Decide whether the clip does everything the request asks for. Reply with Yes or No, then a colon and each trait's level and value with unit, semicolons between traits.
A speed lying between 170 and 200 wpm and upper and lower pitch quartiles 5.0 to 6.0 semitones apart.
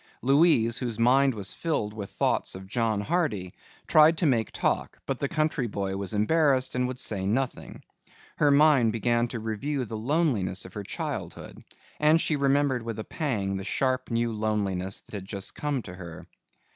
Yes: average, 180 wpm; average, 5.3 semitones